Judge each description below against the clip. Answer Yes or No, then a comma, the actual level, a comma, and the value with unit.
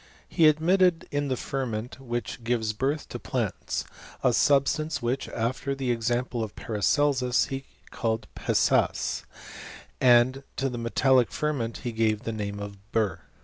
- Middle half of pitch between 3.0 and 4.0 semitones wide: Yes, average, 3.3 semitones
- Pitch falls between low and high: No, low, 125 Hz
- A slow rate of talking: No, average, 145 wpm